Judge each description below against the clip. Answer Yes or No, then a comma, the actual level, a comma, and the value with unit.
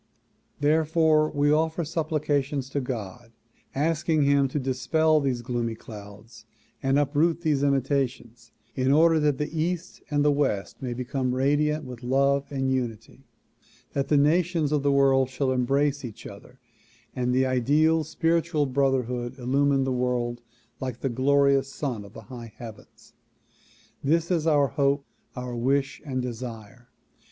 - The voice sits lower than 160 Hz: Yes, low, 135 Hz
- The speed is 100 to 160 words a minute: Yes, average, 145 wpm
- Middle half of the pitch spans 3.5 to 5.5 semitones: No, average, 3.0 semitones